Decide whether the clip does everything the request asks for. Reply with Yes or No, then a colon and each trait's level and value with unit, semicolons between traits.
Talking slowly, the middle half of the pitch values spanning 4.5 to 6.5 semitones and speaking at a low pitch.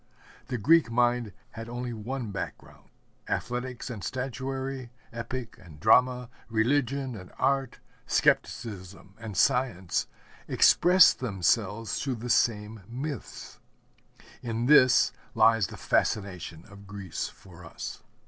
No: slow, 110 wpm; average, 3.8 semitones; low, 115 Hz